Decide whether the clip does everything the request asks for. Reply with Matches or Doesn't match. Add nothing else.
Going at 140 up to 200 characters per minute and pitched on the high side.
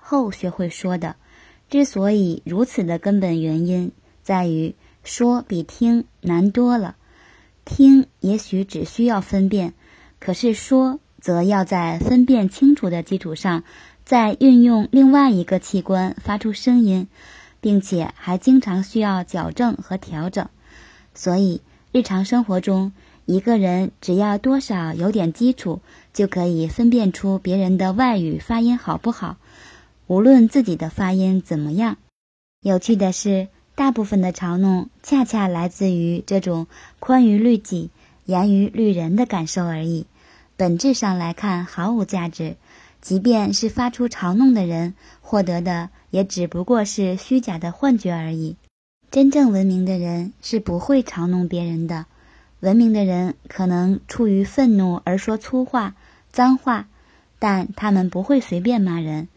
Doesn't match